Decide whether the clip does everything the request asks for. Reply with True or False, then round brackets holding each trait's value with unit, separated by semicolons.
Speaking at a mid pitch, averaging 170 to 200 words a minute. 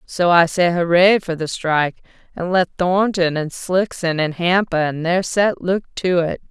True (175 Hz; 185 wpm)